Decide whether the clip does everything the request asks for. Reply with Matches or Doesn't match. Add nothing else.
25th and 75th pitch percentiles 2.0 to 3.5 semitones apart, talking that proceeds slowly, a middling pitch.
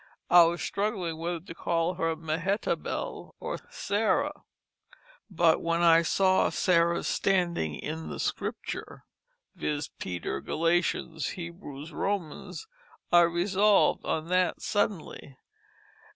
Matches